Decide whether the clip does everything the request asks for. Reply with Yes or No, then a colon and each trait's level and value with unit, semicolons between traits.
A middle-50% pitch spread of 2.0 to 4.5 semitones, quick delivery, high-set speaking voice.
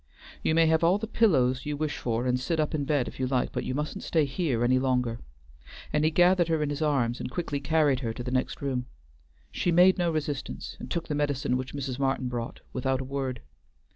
No: average, 3.7 semitones; fast, 230 wpm; medium, 140 Hz